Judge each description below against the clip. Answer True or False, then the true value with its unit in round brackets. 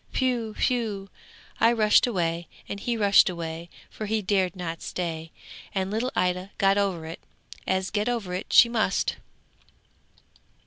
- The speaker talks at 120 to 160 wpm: True (145 wpm)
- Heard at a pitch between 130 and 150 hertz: False (195 Hz)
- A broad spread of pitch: False (3.5 semitones)